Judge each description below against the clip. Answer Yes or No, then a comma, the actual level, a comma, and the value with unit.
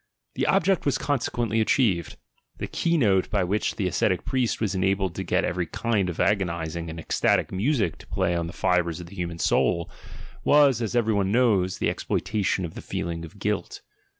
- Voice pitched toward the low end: Yes, very low, 95 Hz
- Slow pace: No, average, 190 wpm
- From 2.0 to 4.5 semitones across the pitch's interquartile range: No, average, 4.9 semitones